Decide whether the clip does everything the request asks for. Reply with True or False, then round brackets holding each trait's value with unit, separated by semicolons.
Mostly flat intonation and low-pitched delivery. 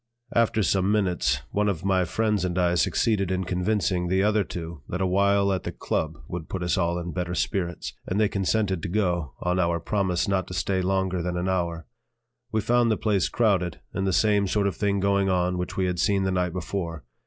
True (2.2 semitones; 95 Hz)